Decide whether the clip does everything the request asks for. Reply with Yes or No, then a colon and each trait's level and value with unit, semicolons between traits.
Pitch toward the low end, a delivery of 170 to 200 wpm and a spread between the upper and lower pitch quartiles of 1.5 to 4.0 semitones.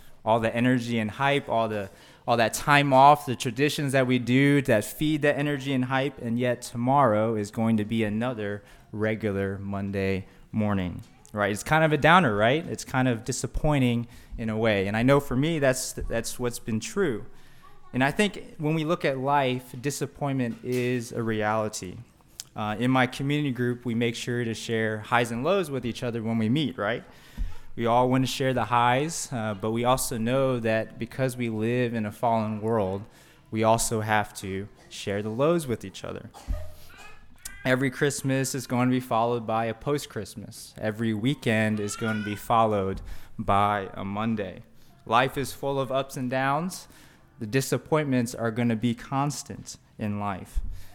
Yes: low, 120 Hz; average, 185 wpm; average, 3.5 semitones